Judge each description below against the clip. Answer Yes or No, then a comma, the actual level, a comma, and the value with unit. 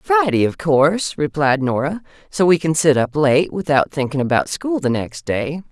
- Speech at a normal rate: Yes, average, 190 wpm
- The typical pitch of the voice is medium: Yes, medium, 155 Hz